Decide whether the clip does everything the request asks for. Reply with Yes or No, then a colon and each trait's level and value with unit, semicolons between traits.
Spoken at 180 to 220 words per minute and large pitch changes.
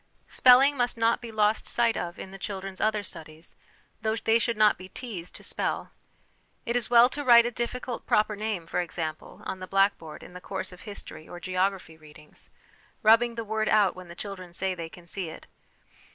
No: average, 200 wpm; average, 4.3 semitones